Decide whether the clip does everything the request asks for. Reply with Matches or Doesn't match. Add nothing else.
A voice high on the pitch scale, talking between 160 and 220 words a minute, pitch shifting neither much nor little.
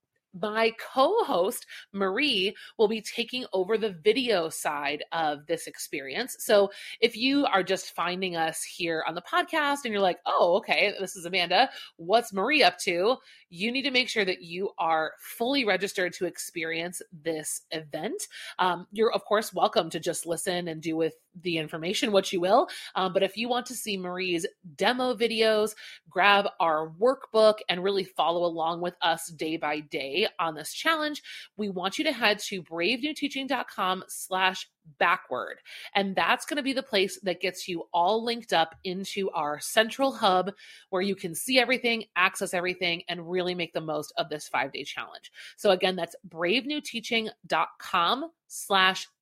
Matches